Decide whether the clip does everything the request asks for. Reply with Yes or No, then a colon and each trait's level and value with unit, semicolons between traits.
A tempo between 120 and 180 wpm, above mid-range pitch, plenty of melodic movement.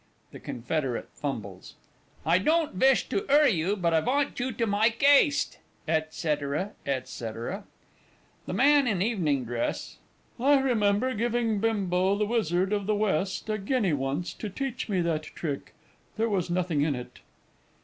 Yes: average, 150 wpm; high, 195 Hz; wide, 6.7 semitones